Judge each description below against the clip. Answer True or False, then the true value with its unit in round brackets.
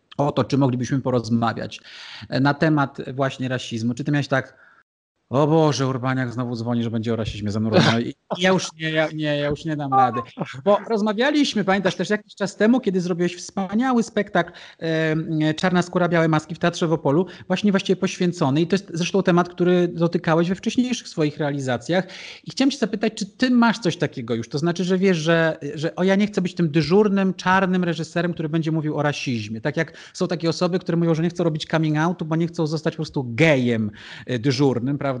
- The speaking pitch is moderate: True (165 Hz)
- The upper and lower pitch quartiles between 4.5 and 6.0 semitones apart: True (4.8 semitones)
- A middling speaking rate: False (205 wpm)